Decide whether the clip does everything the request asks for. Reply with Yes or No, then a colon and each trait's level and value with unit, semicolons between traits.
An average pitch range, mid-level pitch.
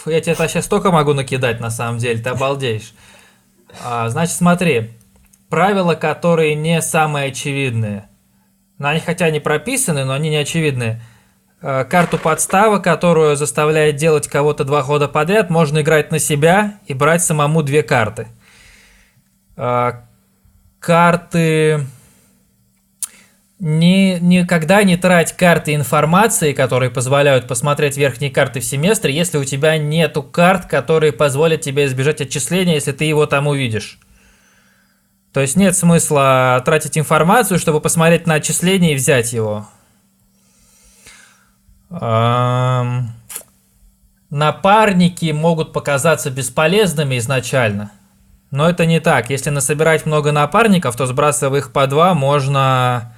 Yes: average, 4.0 semitones; medium, 150 Hz